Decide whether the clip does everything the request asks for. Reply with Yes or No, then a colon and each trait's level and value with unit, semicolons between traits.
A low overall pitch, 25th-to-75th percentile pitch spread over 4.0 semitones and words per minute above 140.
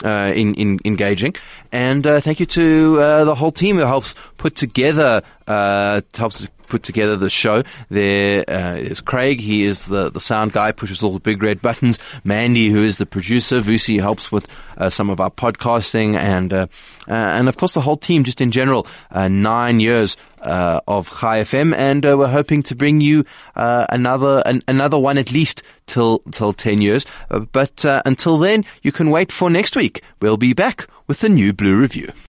Yes: low, 120 Hz; average, 5.2 semitones; fast, 205 wpm